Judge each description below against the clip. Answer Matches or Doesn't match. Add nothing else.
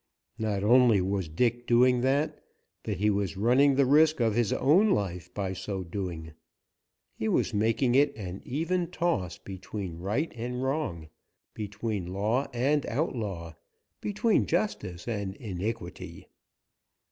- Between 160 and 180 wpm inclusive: Doesn't match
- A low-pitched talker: Matches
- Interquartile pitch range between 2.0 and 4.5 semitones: Doesn't match